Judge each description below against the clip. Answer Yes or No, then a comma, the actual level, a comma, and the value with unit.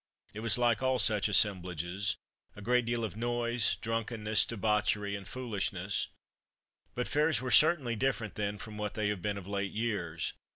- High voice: No, low, 110 Hz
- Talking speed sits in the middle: Yes, average, 165 wpm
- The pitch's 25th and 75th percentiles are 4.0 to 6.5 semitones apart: No, average, 2.9 semitones